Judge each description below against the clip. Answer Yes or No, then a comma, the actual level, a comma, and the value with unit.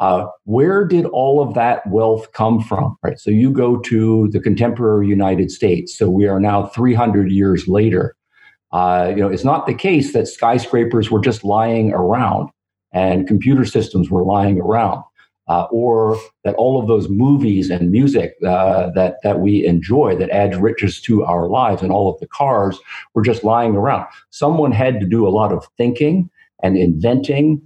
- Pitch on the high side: No, low, 110 Hz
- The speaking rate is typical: Yes, average, 180 wpm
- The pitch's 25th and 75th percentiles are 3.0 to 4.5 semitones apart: Yes, average, 3.6 semitones